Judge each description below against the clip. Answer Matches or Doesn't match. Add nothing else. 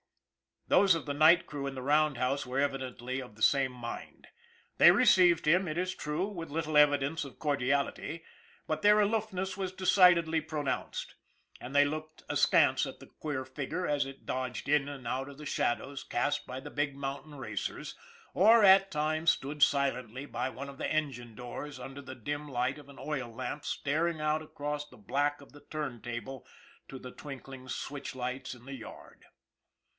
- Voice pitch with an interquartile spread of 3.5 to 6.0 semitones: Doesn't match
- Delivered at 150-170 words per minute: Doesn't match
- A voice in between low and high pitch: Matches